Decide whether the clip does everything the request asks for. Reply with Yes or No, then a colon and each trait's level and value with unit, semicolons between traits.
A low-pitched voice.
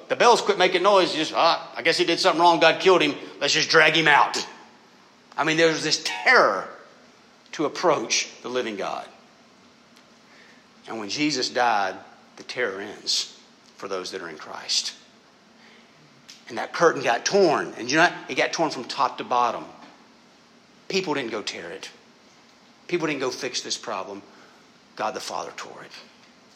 No: medium, 160 Hz